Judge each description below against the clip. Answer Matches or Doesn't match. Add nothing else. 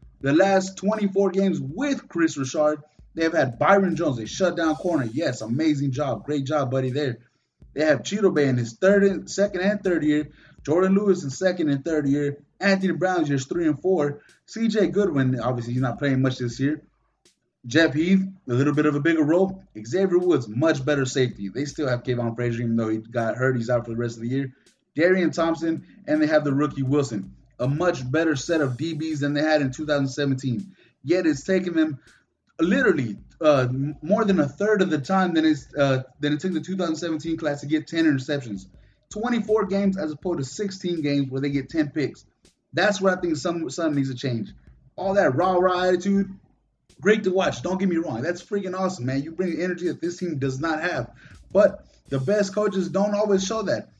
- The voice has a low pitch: Doesn't match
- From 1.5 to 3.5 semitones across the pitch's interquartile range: Doesn't match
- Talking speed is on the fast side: Matches